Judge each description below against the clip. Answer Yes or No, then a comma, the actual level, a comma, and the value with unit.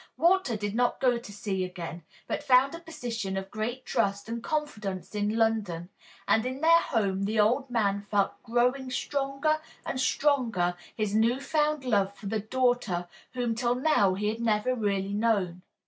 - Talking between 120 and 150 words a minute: No, average, 170 wpm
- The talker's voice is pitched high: Yes, high, 225 Hz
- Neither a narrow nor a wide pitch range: Yes, average, 4.2 semitones